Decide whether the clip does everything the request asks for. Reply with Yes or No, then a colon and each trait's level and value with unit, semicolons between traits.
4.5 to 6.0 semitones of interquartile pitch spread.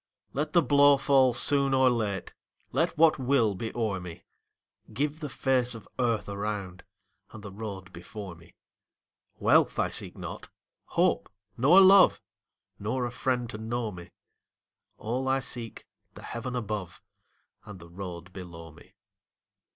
Yes: average, 5.1 semitones